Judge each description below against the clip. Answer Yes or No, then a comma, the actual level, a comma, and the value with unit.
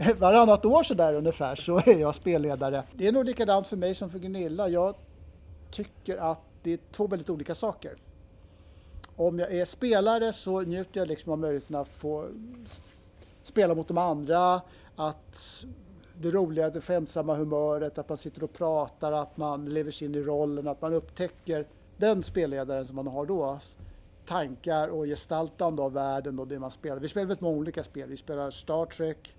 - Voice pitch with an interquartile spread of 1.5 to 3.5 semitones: No, average, 4.5 semitones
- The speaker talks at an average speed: Yes, average, 180 wpm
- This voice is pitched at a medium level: Yes, medium, 155 Hz